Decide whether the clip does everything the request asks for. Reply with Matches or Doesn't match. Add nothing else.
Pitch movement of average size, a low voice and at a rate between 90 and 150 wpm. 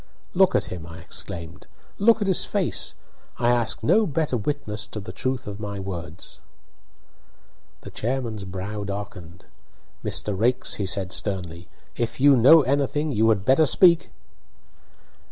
Doesn't match